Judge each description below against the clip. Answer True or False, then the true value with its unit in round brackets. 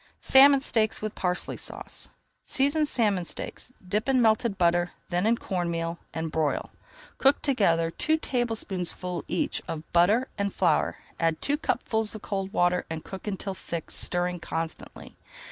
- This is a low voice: False (190 Hz)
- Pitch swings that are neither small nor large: True (4.9 semitones)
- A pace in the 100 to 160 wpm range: True (150 wpm)